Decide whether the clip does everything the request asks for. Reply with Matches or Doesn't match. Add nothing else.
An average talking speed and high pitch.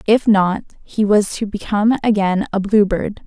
Matches